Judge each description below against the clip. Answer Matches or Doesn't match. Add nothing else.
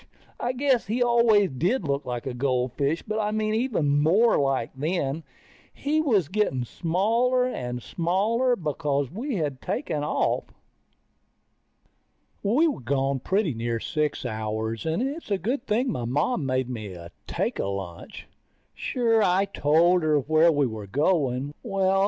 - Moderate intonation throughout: Doesn't match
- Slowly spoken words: Doesn't match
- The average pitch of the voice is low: Doesn't match